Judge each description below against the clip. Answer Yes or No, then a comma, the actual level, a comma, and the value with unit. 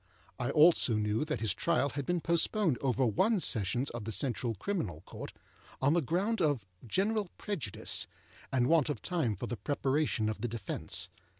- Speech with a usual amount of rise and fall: No, wide, 7.1 semitones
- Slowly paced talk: No, average, 175 wpm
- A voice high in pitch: No, low, 135 Hz